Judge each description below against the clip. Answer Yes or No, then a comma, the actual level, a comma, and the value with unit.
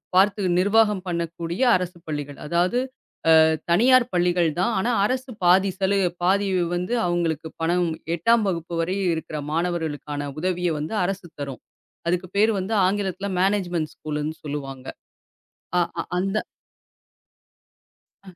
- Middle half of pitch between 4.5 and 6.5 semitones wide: No, average, 3.3 semitones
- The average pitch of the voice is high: No, medium, 180 Hz